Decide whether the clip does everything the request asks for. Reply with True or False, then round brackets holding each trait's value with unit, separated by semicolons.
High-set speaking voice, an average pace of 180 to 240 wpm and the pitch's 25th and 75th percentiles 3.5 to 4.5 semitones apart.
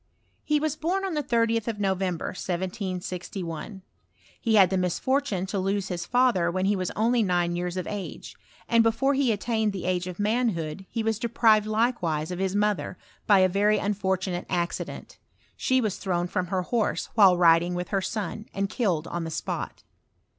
True (195 Hz; 185 wpm; 3.9 semitones)